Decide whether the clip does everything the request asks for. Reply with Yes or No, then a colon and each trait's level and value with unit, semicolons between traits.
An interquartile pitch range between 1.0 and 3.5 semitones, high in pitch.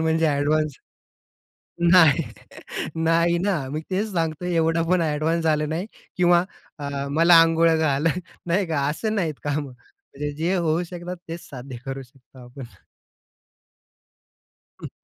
No: average, 2.8 semitones; medium, 160 Hz